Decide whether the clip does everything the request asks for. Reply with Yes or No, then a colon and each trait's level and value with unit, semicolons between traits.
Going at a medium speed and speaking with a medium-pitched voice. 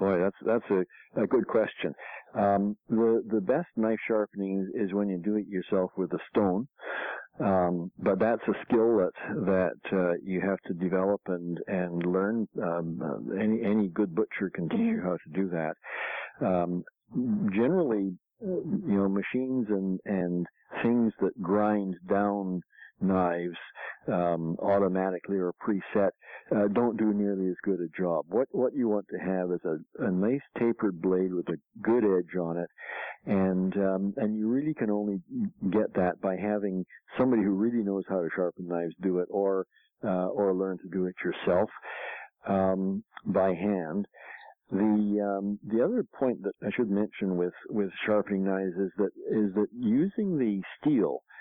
No: average, 165 wpm; low, 100 Hz